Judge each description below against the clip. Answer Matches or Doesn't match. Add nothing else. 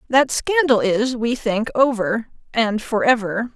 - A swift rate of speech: Doesn't match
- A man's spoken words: Doesn't match